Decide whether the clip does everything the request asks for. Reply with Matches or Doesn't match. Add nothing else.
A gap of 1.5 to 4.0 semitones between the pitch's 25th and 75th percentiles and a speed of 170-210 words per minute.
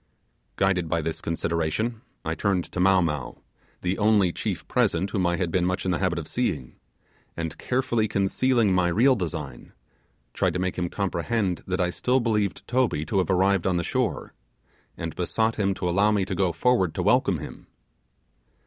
Matches